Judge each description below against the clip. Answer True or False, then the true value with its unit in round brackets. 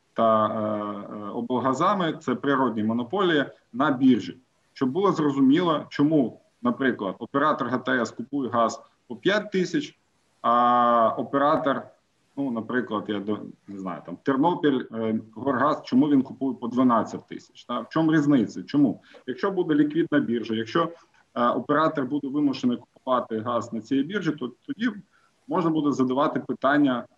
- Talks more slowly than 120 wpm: False (140 wpm)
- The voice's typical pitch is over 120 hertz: True (135 Hz)